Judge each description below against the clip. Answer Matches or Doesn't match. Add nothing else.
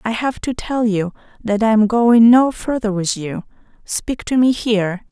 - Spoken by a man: Doesn't match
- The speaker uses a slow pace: Doesn't match